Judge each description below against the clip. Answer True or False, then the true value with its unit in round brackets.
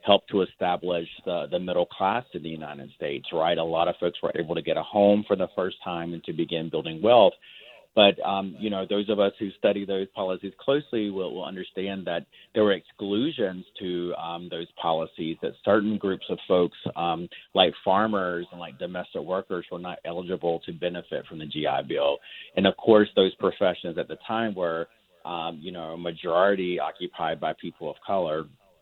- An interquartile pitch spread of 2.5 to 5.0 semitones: True (2.9 semitones)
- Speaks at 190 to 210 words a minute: True (195 wpm)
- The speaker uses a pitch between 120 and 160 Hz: False (90 Hz)